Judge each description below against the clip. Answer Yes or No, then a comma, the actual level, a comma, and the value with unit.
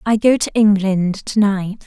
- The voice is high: Yes, high, 205 Hz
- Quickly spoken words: No, average, 195 wpm